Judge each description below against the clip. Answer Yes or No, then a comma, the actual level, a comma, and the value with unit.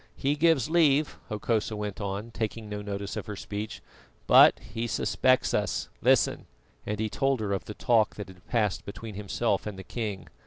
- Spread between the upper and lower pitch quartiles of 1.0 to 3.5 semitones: Yes, narrow, 2.6 semitones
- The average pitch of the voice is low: Yes, low, 105 Hz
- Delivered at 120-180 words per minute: No, average, 190 wpm